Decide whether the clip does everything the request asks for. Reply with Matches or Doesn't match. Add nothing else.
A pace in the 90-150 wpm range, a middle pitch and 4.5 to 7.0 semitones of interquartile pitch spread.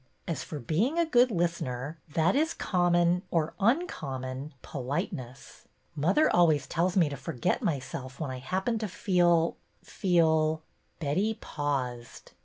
Doesn't match